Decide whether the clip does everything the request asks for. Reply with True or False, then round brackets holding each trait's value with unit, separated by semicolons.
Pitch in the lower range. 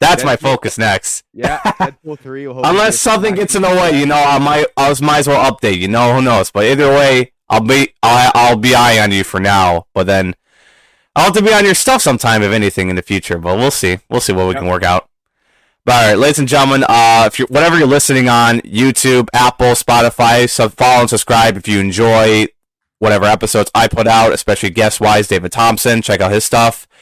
True (120 Hz)